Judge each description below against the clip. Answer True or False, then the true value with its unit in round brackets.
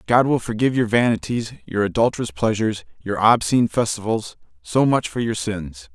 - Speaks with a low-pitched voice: True (110 Hz)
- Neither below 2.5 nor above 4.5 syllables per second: False (5.6 syllables/s)